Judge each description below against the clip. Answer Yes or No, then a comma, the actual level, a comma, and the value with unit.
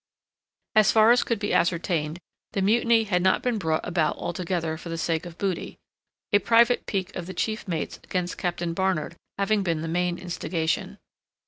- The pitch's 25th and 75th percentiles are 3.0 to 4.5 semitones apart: Yes, average, 3.5 semitones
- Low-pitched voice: No, medium, 180 Hz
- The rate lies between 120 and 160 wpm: No, average, 180 wpm